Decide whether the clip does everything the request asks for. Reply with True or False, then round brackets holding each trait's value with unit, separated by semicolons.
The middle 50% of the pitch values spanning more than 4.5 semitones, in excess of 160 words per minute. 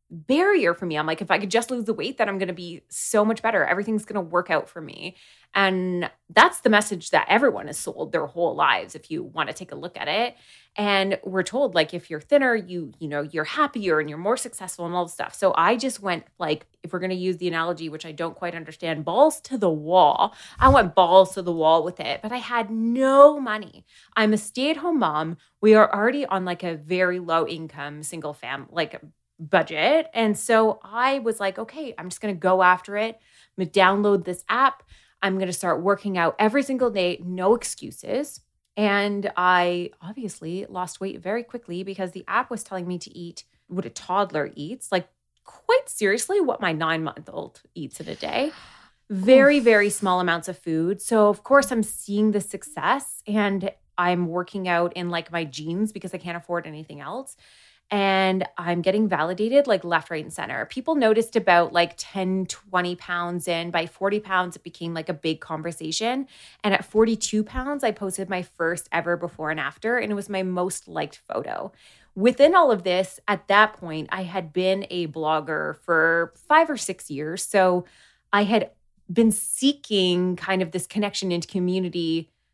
False (3.9 semitones; 205 wpm)